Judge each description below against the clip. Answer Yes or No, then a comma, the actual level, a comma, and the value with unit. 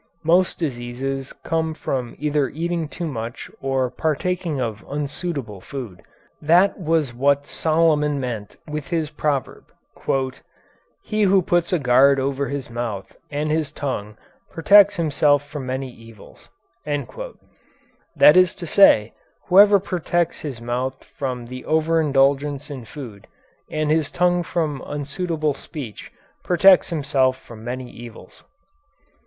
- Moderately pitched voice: Yes, medium, 145 Hz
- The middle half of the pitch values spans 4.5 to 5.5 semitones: No, average, 4.1 semitones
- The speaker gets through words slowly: Yes, slow, 125 wpm